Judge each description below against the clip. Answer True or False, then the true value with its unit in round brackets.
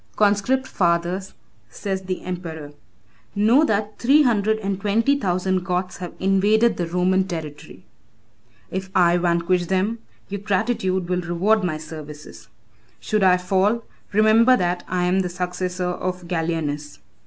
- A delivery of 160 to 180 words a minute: False (135 wpm)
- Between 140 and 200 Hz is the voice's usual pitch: True (185 Hz)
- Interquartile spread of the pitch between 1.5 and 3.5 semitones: True (2.8 semitones)